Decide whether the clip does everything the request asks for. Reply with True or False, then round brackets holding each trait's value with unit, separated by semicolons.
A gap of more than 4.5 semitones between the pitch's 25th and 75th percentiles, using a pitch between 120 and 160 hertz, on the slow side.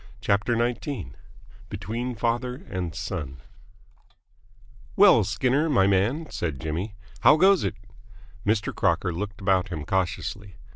False (5.0 semitones; 105 Hz; 115 wpm)